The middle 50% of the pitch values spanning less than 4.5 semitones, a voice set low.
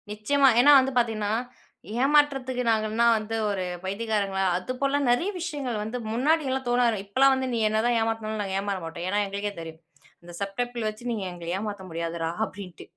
No: average, 4.1 semitones; high, 220 Hz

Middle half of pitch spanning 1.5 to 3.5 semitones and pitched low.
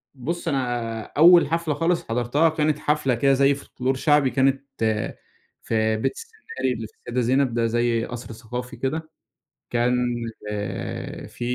No: average, 3.9 semitones; low, 130 Hz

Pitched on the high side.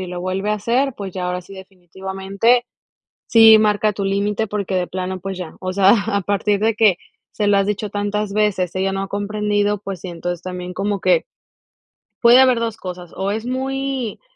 Yes: high, 200 Hz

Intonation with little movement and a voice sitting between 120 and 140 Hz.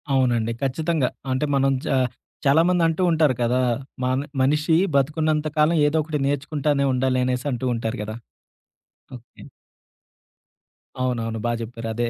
No: average, 3.5 semitones; low, 135 Hz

